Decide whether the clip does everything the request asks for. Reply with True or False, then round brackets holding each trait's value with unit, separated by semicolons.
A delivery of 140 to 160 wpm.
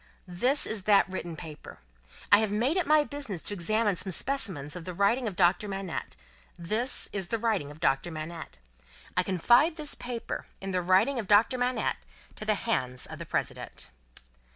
False (180 wpm)